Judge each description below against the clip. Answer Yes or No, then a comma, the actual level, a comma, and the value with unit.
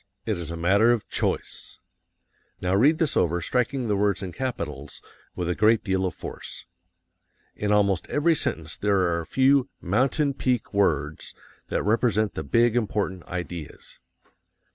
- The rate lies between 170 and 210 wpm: No, average, 155 wpm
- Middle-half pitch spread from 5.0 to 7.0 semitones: Yes, wide, 5.5 semitones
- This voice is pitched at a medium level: No, low, 100 Hz